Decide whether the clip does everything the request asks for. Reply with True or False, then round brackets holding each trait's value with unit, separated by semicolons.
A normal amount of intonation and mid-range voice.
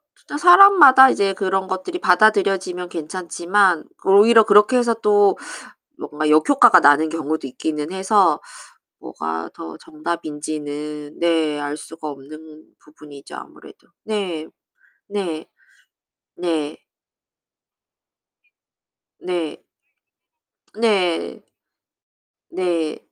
True (4.7 semitones; 170 Hz)